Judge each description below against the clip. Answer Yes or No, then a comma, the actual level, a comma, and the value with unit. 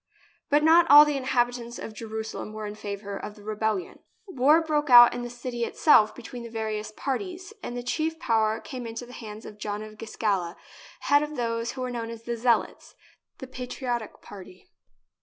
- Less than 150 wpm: No, average, 195 wpm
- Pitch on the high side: Yes, high, 235 Hz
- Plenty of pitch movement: No, average, 3.3 semitones